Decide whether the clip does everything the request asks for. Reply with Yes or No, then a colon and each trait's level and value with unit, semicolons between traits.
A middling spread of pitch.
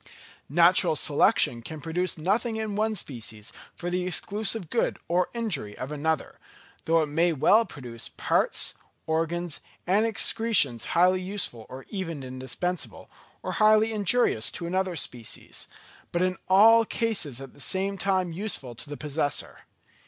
No: wide, 5.8 semitones